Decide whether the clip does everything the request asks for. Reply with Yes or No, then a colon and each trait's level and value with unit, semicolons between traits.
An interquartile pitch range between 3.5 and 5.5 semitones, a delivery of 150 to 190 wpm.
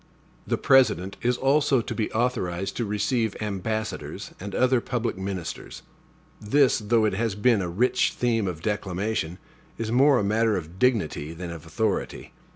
Yes: average, 4.2 semitones; average, 160 wpm